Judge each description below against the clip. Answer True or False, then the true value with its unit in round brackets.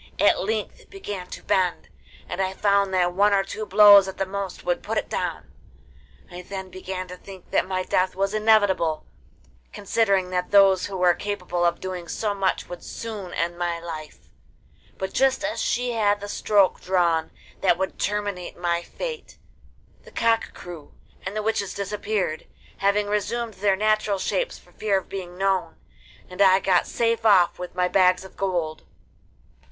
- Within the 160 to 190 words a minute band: True (175 wpm)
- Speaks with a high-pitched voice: True (195 Hz)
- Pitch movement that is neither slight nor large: False (2.3 semitones)